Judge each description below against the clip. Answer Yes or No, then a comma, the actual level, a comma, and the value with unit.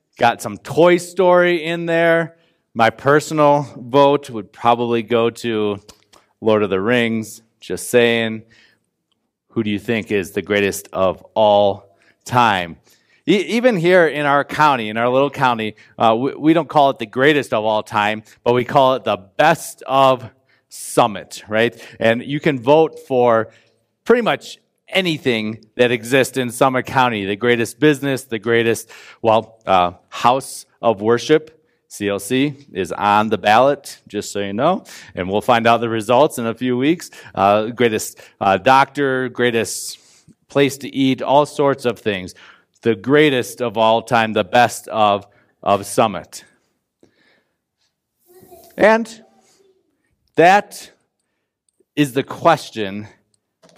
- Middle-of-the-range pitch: No, low, 120 Hz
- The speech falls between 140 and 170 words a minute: Yes, average, 145 wpm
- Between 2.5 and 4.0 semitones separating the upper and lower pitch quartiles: No, average, 4.6 semitones